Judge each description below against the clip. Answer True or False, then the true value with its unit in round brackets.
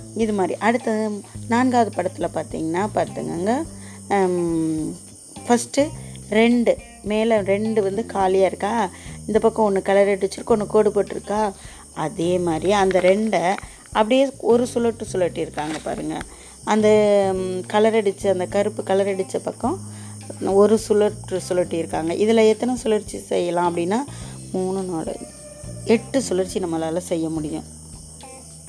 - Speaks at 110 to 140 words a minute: True (115 wpm)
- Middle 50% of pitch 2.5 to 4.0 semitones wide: False (4.8 semitones)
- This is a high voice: True (195 Hz)